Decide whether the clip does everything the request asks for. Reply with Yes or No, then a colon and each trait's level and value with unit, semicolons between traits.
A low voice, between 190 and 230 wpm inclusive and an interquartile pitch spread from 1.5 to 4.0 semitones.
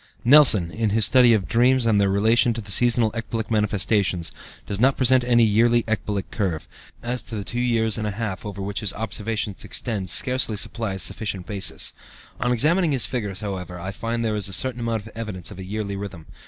Yes: low, 110 Hz; average, 200 wpm; average, 2.9 semitones